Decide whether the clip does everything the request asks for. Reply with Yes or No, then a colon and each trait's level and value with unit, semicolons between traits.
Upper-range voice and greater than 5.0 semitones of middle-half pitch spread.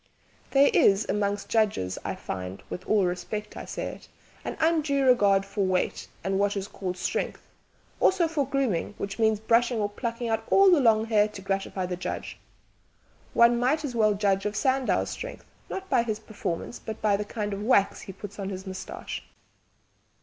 No: high, 210 Hz; average, 3.6 semitones